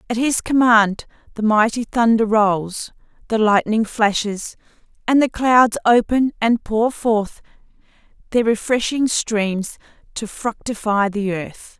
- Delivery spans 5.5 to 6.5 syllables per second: No, 3.8 syllables/s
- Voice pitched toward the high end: Yes, high, 220 Hz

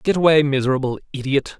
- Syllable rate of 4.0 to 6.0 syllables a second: No, 6.6 syllables/s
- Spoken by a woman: No, male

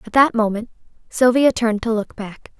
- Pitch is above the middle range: Yes, high, 230 Hz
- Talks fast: No, average, 185 wpm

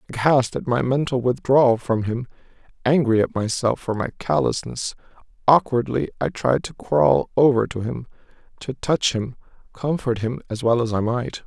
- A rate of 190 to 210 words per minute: No, average, 160 wpm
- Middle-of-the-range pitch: No, low, 125 Hz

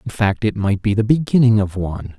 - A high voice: No, low, 105 Hz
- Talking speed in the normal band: No, fast, 245 wpm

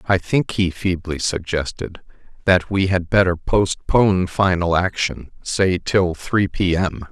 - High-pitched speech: No, very low, 90 Hz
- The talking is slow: No, average, 145 wpm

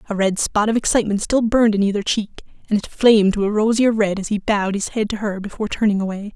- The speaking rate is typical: No, fast, 255 wpm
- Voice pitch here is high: Yes, high, 210 Hz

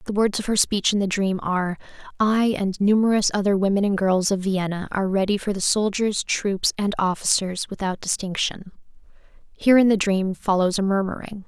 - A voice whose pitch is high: Yes, high, 200 Hz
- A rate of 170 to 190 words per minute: Yes, average, 185 wpm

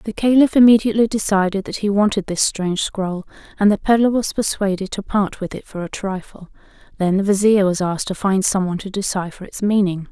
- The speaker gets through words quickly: Yes, fast, 210 wpm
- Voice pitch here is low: No, high, 200 Hz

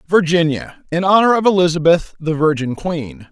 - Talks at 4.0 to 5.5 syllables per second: Yes, 4.9 syllables/s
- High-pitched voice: No, medium, 170 Hz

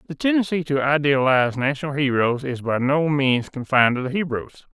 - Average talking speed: Yes, average, 175 wpm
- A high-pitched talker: No, medium, 140 Hz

